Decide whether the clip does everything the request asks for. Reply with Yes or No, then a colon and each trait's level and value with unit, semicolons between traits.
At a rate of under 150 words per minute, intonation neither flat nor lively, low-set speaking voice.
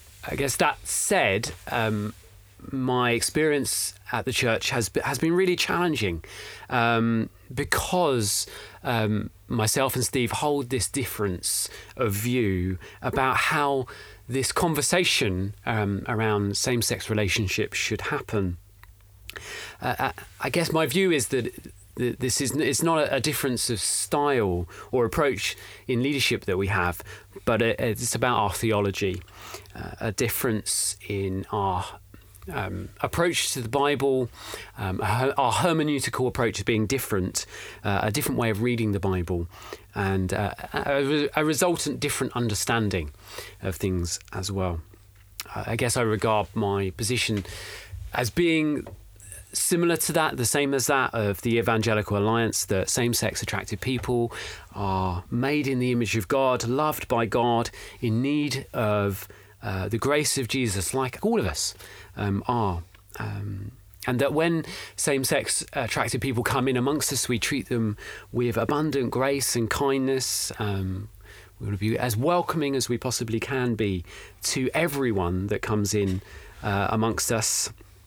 Yes: average, 140 wpm; average, 4.8 semitones; low, 115 Hz